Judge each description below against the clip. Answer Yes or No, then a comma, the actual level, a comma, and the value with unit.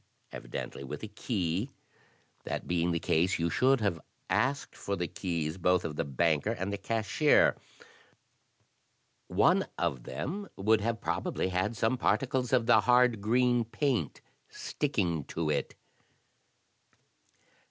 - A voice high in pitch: No, low, 100 Hz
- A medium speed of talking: No, slow, 130 wpm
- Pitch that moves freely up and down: Yes, wide, 6.4 semitones